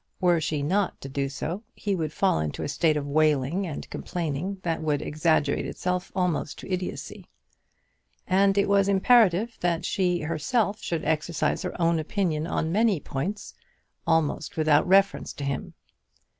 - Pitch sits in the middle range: Yes, medium, 170 Hz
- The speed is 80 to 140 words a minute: No, average, 155 wpm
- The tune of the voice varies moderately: Yes, average, 4.0 semitones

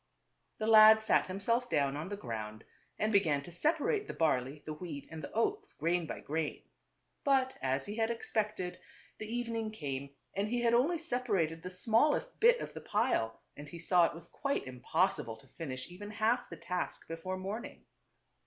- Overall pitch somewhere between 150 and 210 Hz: Yes, high, 190 Hz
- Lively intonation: Yes, wide, 7.0 semitones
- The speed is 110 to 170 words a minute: No, average, 180 wpm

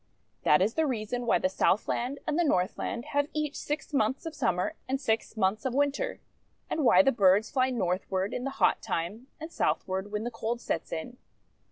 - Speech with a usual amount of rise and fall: No, wide, 6.1 semitones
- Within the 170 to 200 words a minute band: Yes, average, 195 wpm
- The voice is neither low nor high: No, high, 240 Hz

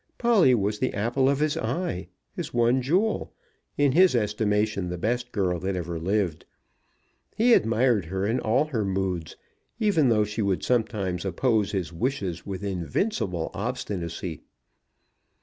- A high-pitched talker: No, low, 105 Hz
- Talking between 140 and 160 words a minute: Yes, average, 145 wpm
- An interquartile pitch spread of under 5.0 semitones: No, wide, 5.4 semitones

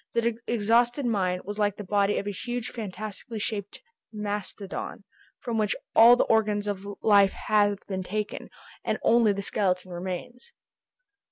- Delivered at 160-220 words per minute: No, average, 150 wpm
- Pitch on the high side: Yes, high, 210 Hz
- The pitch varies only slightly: Yes, narrow, 2.2 semitones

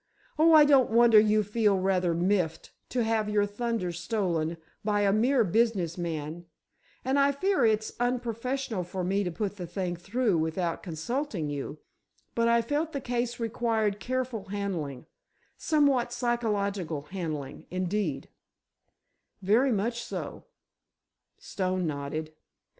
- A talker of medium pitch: No, high, 205 Hz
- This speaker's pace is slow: Yes, slow, 125 wpm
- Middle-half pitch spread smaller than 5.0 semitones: No, average, 5.3 semitones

